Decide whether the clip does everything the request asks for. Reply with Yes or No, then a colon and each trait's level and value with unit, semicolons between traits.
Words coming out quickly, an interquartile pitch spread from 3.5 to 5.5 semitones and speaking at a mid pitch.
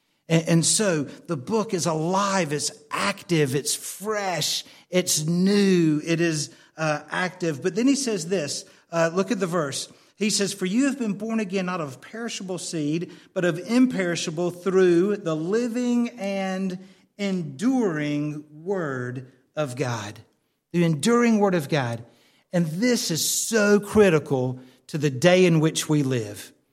No: average, 150 wpm; average, 4.7 semitones; medium, 175 Hz